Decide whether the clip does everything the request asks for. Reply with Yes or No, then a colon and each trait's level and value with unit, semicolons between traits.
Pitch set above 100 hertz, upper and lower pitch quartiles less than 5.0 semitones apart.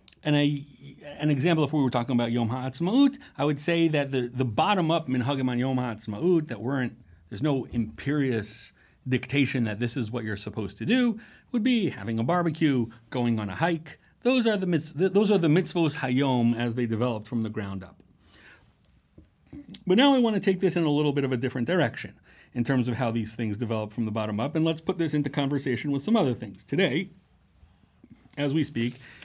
No: low, 135 Hz; wide, 5.6 semitones